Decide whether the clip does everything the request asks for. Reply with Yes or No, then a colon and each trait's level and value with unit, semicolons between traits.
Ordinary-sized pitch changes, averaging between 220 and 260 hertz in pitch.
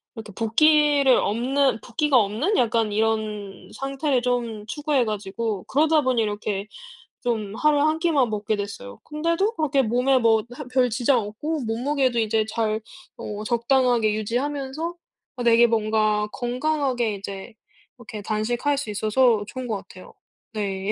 Yes: average, 4.2 semitones; high, 235 Hz